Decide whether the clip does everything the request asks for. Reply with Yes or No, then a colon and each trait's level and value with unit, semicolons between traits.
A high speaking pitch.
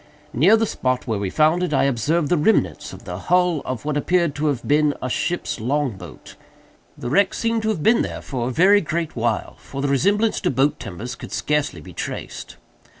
No: medium, 150 Hz